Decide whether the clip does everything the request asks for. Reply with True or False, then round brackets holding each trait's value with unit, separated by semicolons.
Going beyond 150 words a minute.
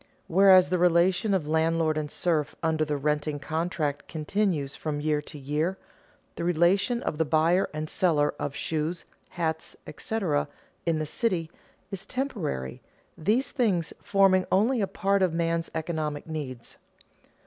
False (145 wpm)